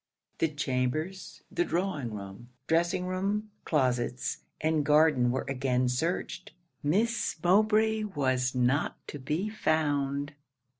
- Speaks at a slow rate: Yes, slow, 110 wpm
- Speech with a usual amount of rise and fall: No, wide, 6.2 semitones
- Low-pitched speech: No, medium, 150 Hz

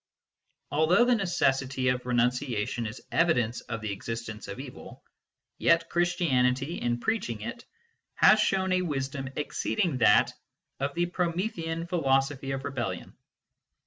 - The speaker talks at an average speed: No, slow, 125 wpm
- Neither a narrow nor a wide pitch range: No, wide, 5.7 semitones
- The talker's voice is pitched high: No, low, 135 Hz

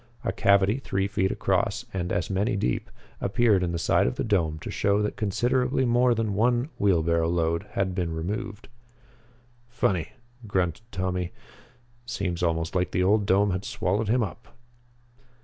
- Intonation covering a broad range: No, average, 3.8 semitones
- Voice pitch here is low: Yes, low, 100 Hz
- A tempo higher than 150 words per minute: Yes, average, 160 wpm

